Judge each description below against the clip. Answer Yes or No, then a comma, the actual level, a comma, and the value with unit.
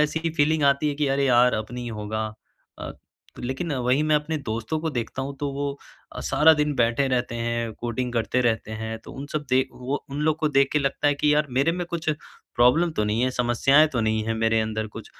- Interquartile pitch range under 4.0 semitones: No, average, 4.3 semitones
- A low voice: Yes, low, 130 Hz